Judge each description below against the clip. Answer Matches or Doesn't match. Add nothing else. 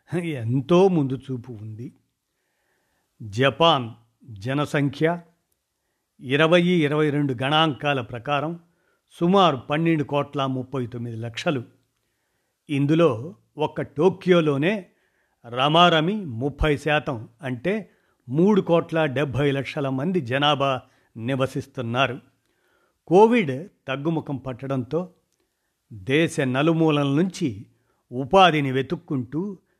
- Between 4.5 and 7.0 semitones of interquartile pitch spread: Doesn't match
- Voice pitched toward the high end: Doesn't match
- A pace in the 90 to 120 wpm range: Doesn't match